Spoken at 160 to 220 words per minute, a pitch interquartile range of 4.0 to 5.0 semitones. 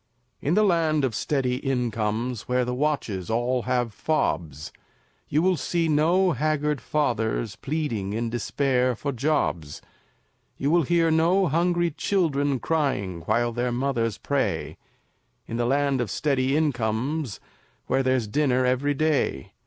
No: slow, 135 wpm; average, 4.5 semitones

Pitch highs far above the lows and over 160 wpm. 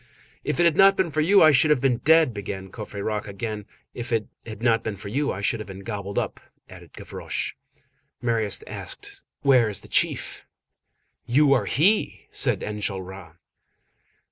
Yes: wide, 6.2 semitones; average, 170 wpm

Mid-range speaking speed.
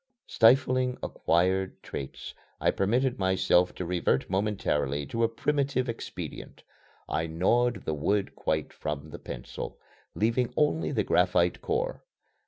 No: slow, 125 wpm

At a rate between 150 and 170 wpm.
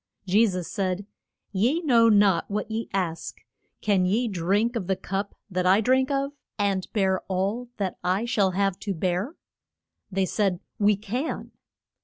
Yes: average, 160 wpm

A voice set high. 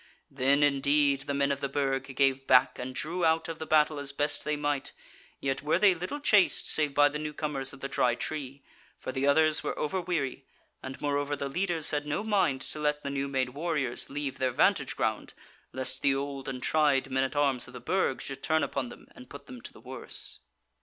No: medium, 140 Hz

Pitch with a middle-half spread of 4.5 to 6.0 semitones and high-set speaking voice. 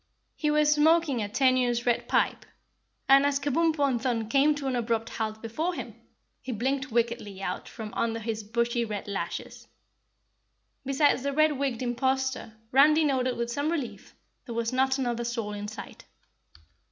No: average, 3.5 semitones; very high, 255 Hz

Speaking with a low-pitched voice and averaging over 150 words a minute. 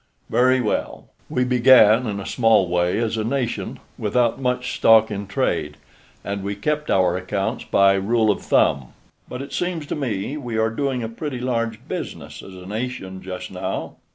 Yes: low, 115 Hz; average, 180 wpm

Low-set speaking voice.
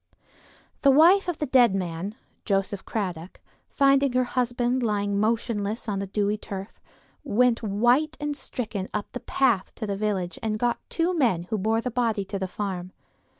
No: high, 220 Hz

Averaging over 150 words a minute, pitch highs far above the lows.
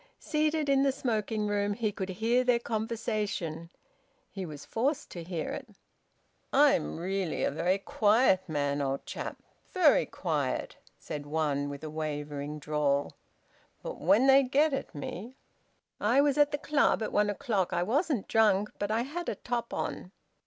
Yes: average, 160 wpm; wide, 7.8 semitones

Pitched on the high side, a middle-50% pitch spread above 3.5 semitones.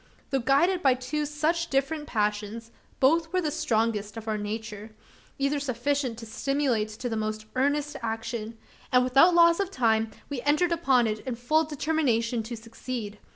Yes: very high, 255 Hz; average, 4.9 semitones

